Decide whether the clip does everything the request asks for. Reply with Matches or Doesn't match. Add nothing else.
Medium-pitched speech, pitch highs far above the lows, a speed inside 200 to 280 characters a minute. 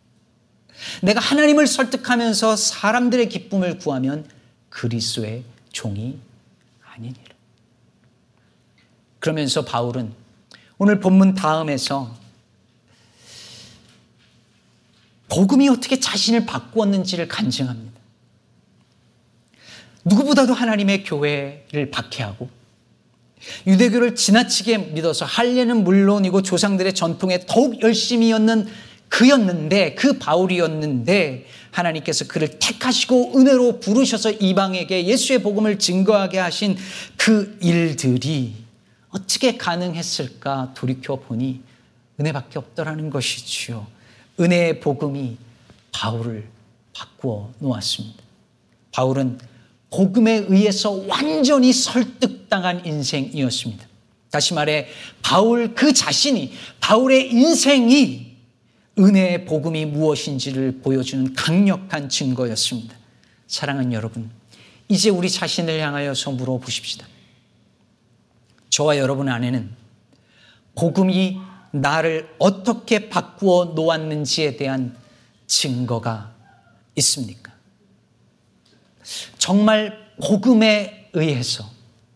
Matches